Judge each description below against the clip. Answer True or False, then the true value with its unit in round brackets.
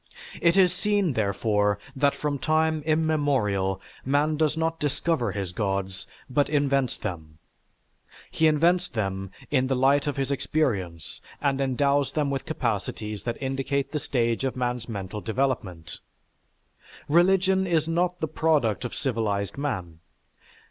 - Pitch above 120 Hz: True (135 Hz)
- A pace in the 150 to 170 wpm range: False (140 wpm)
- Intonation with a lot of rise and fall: True (6.5 semitones)